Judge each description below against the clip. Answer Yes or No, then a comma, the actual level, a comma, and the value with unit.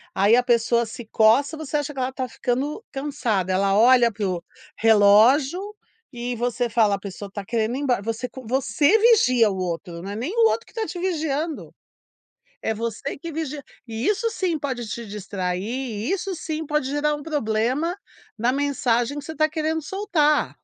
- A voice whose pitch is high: Yes, very high, 255 Hz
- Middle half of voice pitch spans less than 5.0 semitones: No, wide, 5.5 semitones